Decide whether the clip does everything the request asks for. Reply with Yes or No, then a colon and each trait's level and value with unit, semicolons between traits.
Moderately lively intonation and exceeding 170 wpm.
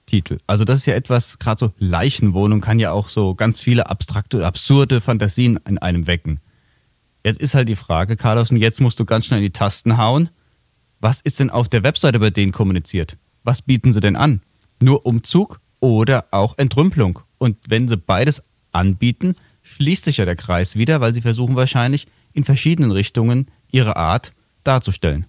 Yes: average, 4.4 semitones; average, 185 wpm